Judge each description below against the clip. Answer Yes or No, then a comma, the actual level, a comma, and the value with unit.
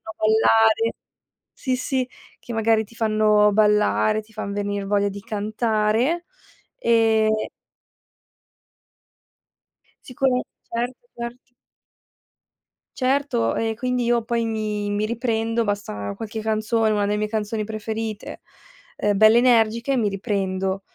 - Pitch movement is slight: Yes, narrow, 1.9 semitones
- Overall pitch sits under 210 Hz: No, high, 220 Hz